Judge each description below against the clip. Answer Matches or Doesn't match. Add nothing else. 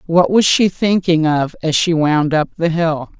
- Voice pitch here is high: Doesn't match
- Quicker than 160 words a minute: Matches